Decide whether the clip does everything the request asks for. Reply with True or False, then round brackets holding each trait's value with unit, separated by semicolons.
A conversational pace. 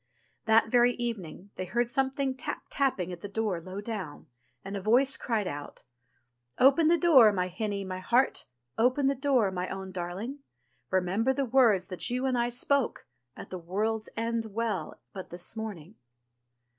True (170 wpm)